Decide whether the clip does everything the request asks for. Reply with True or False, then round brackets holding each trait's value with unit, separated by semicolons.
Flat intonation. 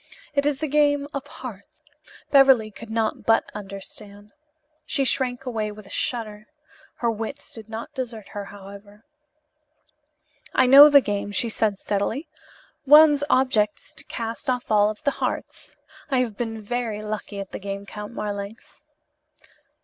False (4.1 semitones)